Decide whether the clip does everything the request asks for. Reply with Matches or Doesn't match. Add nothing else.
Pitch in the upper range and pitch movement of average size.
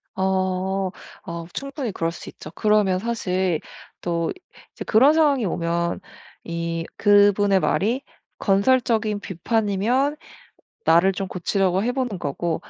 Matches